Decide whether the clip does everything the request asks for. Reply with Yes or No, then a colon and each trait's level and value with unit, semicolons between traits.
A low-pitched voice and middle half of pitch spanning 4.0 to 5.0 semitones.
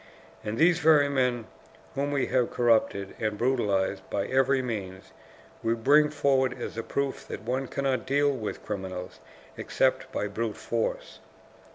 Yes: low, 125 Hz; average, 4.5 semitones